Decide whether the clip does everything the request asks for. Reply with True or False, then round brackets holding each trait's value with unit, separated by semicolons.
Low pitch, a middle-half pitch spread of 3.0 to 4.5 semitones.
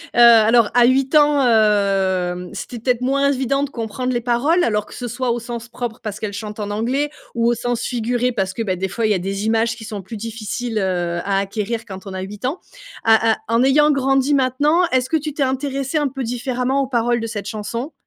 False (235 Hz; 3.7 semitones)